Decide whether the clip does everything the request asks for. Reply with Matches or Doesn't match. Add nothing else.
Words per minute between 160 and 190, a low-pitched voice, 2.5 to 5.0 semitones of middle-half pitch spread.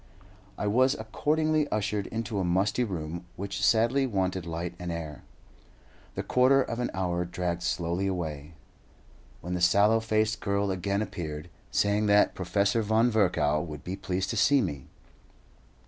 Doesn't match